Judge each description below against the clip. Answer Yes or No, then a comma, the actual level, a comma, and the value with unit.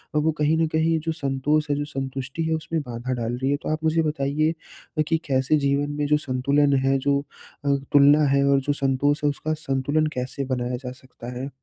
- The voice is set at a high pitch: No, medium, 145 Hz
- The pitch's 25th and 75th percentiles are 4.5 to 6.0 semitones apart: No, narrow, 2.5 semitones